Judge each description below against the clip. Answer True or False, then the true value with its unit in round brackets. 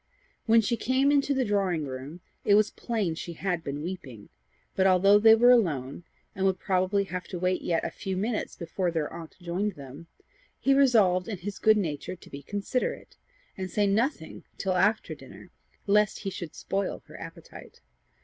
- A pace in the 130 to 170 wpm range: False (180 wpm)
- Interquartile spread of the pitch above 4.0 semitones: False (3.7 semitones)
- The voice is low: False (190 Hz)